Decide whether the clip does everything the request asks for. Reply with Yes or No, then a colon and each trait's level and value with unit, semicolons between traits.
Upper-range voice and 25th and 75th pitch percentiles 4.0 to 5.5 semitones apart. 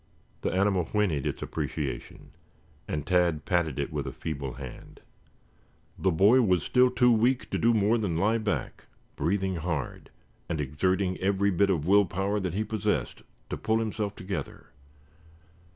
No: very low, 95 Hz; average, 4.5 semitones